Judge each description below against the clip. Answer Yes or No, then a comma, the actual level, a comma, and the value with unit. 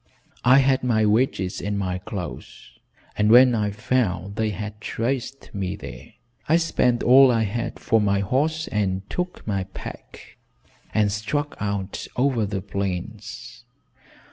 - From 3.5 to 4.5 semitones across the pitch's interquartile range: Yes, average, 4.1 semitones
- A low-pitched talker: Yes, low, 110 Hz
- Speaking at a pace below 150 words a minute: Yes, average, 140 wpm